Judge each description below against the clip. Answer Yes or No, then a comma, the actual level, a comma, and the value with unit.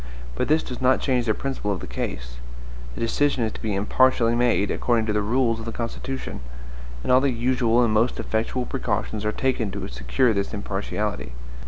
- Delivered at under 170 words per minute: No, average, 195 wpm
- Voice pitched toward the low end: Yes, low, 115 Hz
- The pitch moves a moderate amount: Yes, average, 3.3 semitones